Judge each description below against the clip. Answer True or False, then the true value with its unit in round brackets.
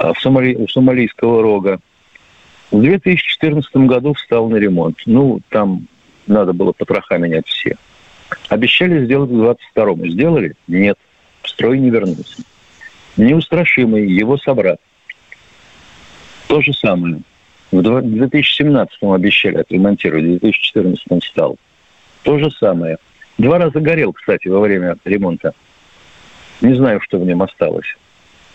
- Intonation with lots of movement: True (6.4 semitones)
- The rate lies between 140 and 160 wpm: False (120 wpm)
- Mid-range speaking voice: False (115 Hz)